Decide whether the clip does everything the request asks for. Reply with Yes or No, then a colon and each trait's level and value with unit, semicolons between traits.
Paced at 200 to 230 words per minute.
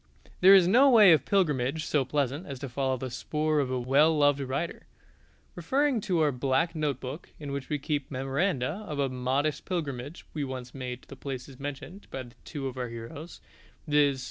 No: average, 190 wpm